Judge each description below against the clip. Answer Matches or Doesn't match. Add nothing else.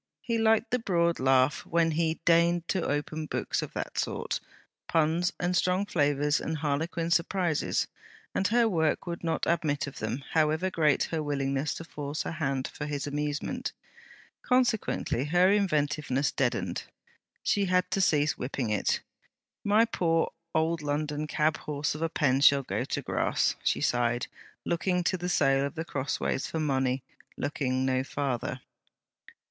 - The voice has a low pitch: Doesn't match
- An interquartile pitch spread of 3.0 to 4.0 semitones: Matches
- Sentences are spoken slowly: Doesn't match